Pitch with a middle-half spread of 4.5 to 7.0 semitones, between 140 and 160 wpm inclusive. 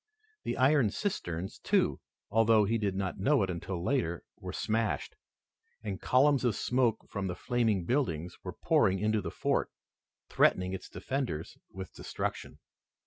Yes: average, 4.9 semitones; average, 145 wpm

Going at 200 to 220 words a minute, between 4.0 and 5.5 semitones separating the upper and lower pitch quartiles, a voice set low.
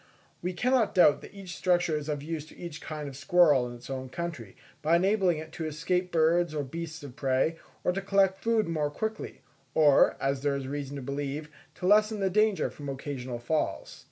No: fast, 205 wpm; average, 4.3 semitones; medium, 155 Hz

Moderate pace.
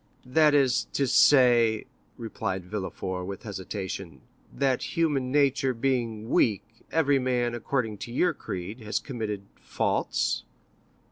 No: slow, 120 wpm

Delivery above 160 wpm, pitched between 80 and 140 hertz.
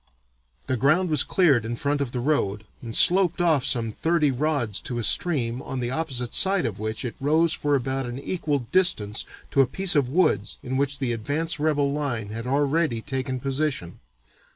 Yes: average, 190 wpm; low, 135 Hz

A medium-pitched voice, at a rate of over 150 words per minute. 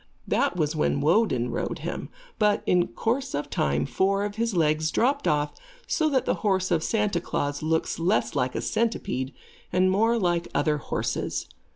Yes: medium, 180 Hz; average, 175 wpm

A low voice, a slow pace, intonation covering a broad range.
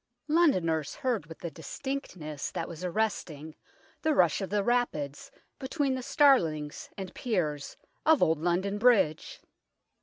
No: medium, 185 Hz; slow, 130 wpm; wide, 8.0 semitones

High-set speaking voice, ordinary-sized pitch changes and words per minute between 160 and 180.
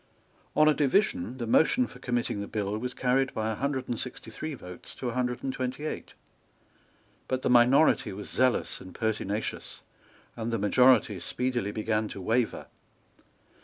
No: low, 120 Hz; average, 3.2 semitones; average, 165 wpm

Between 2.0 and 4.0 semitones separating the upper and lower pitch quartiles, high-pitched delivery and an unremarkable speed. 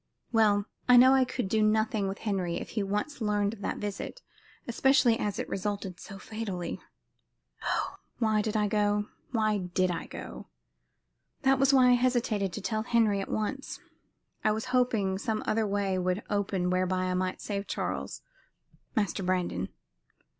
Yes: average, 2.7 semitones; high, 210 Hz; average, 165 wpm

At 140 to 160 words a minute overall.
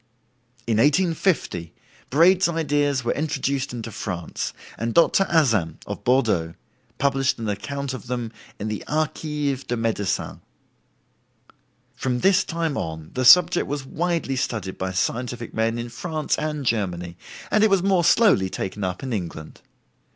Yes: average, 145 wpm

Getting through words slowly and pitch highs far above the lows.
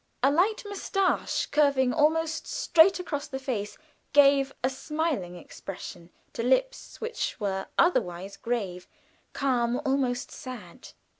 Yes: slow, 120 wpm; wide, 5.7 semitones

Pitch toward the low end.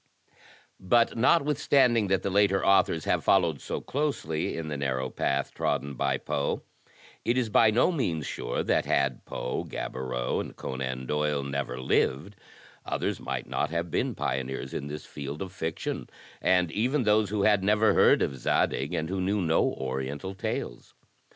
Yes: very low, 80 Hz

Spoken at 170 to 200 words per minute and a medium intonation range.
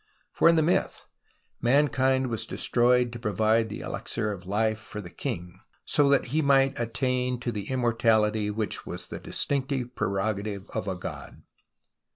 No: average, 160 wpm; average, 3.7 semitones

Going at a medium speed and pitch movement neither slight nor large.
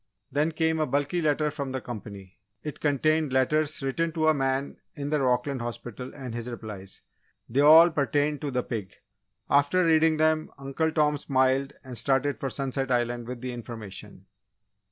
Yes: average, 170 wpm; average, 3.7 semitones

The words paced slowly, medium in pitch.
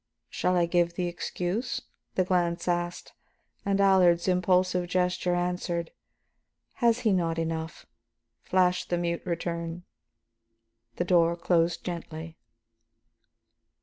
Yes: slow, 110 wpm; medium, 175 Hz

